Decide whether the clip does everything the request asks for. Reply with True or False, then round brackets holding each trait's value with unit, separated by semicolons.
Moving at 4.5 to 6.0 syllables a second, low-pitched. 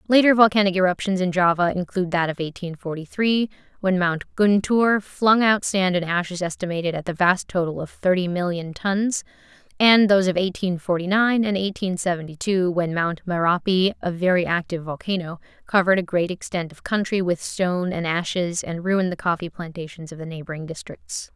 False (5.5 syllables/s; 180 Hz)